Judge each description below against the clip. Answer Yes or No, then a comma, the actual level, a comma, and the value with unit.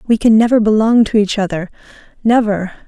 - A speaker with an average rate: Yes, average, 165 wpm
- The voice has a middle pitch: No, high, 215 Hz